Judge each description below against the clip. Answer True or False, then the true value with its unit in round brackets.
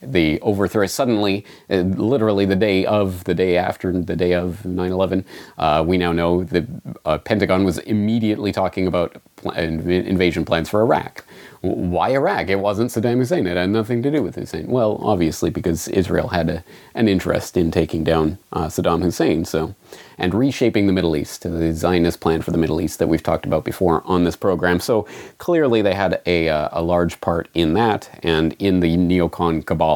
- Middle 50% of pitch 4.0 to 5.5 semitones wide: False (2.8 semitones)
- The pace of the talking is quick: False (190 wpm)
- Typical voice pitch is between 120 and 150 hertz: False (90 Hz)